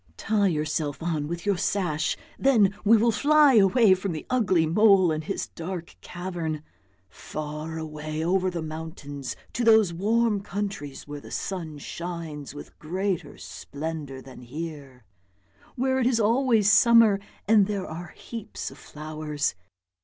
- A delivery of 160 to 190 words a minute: No, average, 145 wpm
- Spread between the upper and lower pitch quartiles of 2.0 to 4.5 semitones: No, average, 5.3 semitones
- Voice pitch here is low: No, medium, 175 Hz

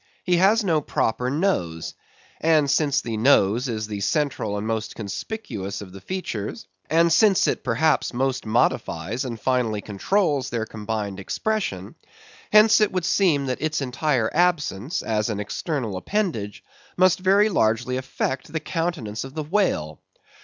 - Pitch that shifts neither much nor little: No, wide, 7.7 semitones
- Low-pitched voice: Yes, low, 130 Hz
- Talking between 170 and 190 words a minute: No, average, 150 wpm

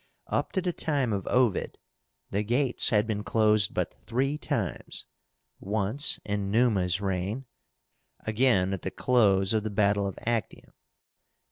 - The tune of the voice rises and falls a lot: No, average, 3.9 semitones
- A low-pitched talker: Yes, low, 110 Hz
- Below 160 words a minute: Yes, average, 140 wpm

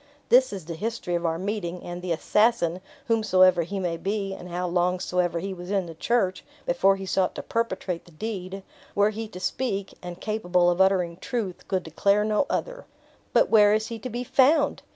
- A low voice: No, high, 190 Hz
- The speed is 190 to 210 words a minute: Yes, average, 200 wpm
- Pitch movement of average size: Yes, average, 3.4 semitones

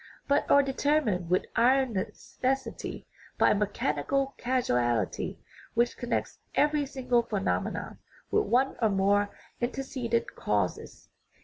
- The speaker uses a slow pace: Yes, slow, 115 wpm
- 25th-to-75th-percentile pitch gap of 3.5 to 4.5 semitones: No, average, 5.0 semitones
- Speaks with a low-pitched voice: No, high, 240 Hz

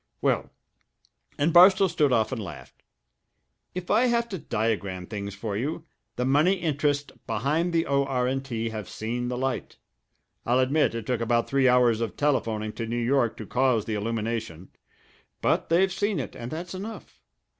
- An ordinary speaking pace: Yes, average, 170 wpm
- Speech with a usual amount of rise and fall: No, wide, 5.7 semitones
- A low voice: Yes, low, 125 Hz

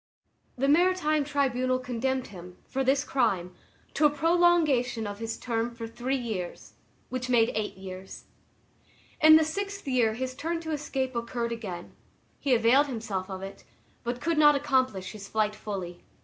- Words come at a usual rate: Yes, average, 160 wpm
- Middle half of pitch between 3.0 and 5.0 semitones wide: Yes, average, 4.7 semitones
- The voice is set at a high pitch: Yes, very high, 250 Hz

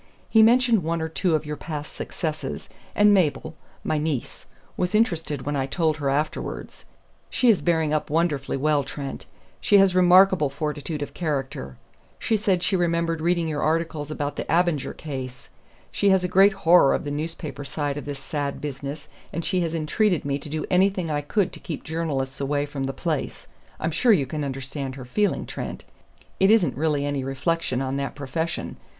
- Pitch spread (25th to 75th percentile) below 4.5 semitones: Yes, average, 3.6 semitones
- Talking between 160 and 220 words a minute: Yes, average, 185 wpm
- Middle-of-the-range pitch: Yes, medium, 155 Hz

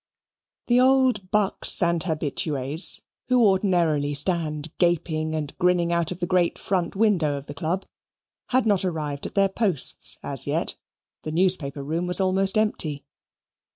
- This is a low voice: No, medium, 175 Hz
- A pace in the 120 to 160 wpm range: Yes, average, 150 wpm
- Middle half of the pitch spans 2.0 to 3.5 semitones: No, average, 3.9 semitones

